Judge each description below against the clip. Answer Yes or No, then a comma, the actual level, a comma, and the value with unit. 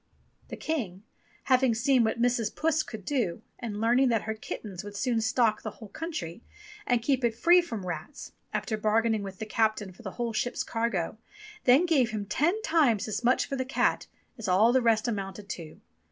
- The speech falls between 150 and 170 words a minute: No, average, 195 wpm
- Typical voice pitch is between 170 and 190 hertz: No, high, 225 Hz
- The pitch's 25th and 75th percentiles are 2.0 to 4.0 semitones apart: Yes, average, 3.4 semitones